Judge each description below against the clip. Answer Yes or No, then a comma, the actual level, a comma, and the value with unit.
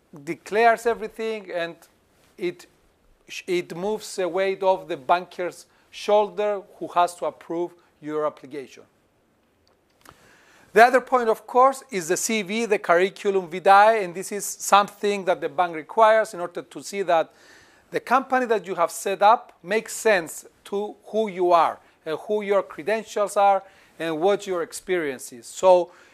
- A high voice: Yes, high, 195 Hz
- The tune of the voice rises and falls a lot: No, average, 3.7 semitones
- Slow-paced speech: No, average, 150 wpm